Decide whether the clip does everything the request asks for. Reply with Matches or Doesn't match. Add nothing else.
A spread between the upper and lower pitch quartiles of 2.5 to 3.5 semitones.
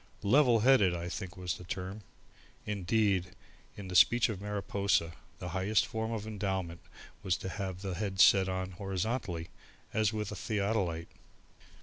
Matches